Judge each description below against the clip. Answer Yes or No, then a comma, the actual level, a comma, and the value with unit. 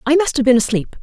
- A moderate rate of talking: No, fast, 295 wpm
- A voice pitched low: No, very high, 275 Hz